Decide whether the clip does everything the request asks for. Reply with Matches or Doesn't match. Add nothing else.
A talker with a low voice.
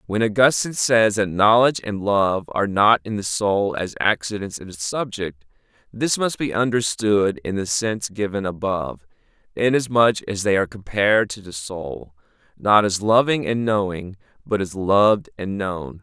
Matches